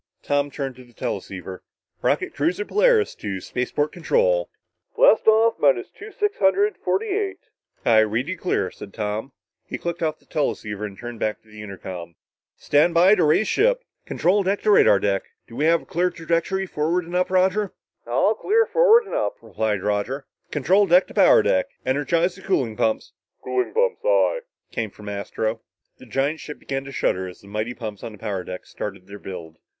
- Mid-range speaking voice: Yes, medium, 145 Hz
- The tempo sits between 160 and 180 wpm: No, average, 190 wpm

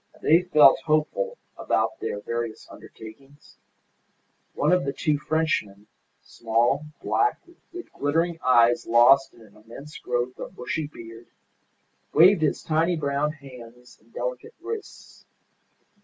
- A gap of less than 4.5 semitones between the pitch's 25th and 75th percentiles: No, average, 5.3 semitones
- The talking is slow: Yes, slow, 125 wpm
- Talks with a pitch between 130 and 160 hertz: Yes, medium, 140 Hz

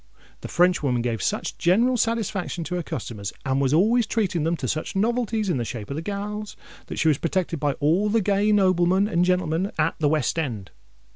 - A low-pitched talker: No, medium, 175 Hz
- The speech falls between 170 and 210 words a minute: Yes, average, 200 wpm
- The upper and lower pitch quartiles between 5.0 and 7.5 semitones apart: Yes, wide, 5.4 semitones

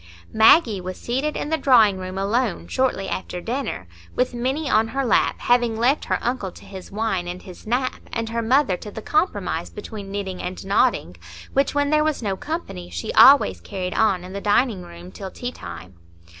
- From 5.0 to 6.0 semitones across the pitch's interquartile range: Yes, wide, 5.5 semitones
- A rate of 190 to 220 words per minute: Yes, average, 195 wpm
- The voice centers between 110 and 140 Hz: No, high, 220 Hz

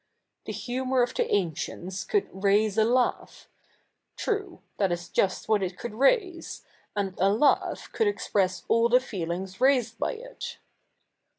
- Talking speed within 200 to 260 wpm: No, average, 155 wpm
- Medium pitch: No, high, 220 Hz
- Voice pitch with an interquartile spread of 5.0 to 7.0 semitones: Yes, wide, 5.5 semitones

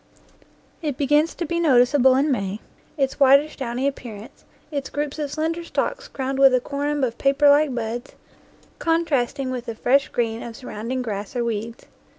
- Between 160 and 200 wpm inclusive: Yes, average, 165 wpm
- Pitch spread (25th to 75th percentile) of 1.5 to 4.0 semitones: Yes, average, 3.4 semitones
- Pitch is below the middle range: No, very high, 270 Hz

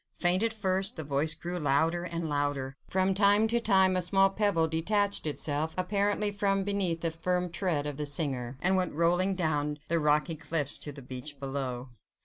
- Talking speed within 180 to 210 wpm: Yes, average, 185 wpm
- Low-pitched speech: No, medium, 170 Hz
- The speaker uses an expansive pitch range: No, average, 4.6 semitones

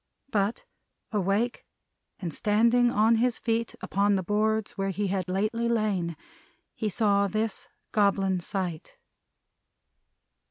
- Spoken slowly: Yes, slow, 115 wpm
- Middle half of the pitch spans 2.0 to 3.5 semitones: Yes, narrow, 2.4 semitones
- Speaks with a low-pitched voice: No, high, 205 Hz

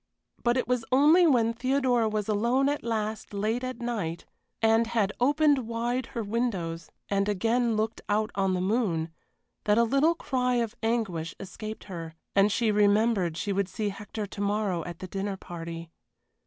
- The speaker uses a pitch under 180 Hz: No, high, 215 Hz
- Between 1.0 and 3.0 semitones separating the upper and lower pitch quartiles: No, average, 3.5 semitones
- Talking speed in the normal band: Yes, average, 170 wpm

